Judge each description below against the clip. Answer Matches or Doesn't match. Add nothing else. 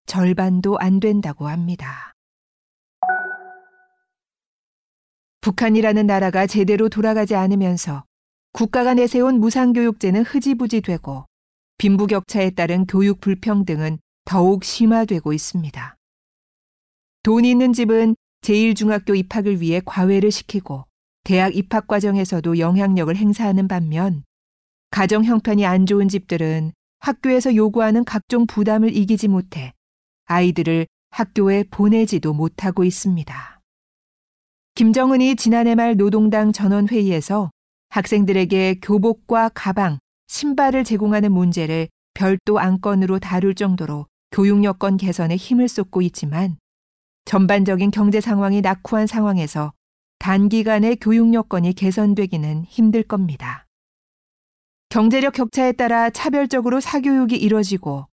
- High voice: Matches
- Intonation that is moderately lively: Matches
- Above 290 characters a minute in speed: Doesn't match